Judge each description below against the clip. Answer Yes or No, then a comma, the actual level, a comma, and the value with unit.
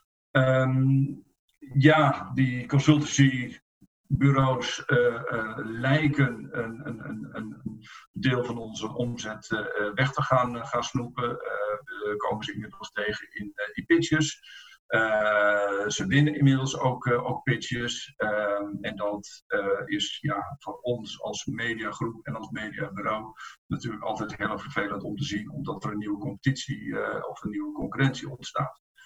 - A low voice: Yes, low, 130 Hz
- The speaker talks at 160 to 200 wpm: No, average, 140 wpm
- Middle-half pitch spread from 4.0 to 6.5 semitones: Yes, average, 4.6 semitones